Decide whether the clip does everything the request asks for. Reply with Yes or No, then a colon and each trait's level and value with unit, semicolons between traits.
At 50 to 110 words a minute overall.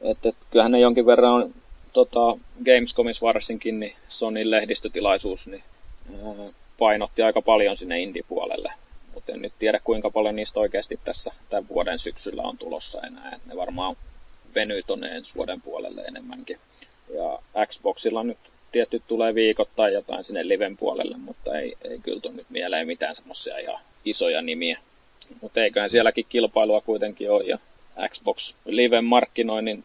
No: fast, 155 wpm